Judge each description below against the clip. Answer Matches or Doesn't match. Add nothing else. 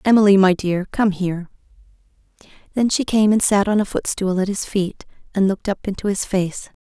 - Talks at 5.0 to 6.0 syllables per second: Matches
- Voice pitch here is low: Doesn't match